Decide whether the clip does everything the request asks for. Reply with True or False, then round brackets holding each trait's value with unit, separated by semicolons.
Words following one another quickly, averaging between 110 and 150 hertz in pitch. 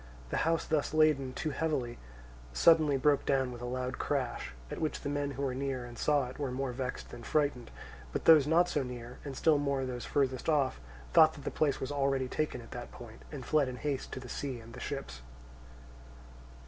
True (210 wpm; 135 Hz)